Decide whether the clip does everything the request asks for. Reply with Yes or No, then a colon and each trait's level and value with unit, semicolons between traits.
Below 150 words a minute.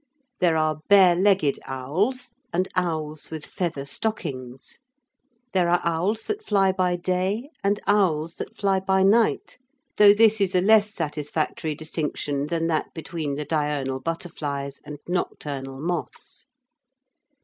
Yes: slow, 135 wpm